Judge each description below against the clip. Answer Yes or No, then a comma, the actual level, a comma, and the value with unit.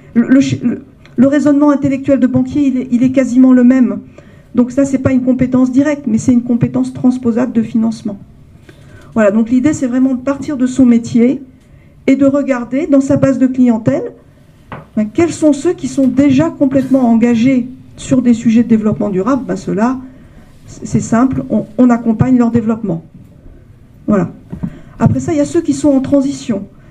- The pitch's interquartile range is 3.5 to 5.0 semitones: No, average, 2.7 semitones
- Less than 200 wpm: Yes, average, 185 wpm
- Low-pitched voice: No, very high, 255 Hz